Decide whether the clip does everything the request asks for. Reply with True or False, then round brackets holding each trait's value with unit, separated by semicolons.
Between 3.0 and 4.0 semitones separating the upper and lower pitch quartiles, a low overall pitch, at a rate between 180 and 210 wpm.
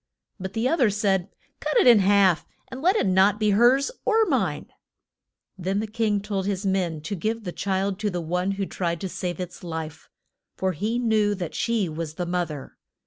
False (3.3 semitones; 195 Hz; 205 wpm)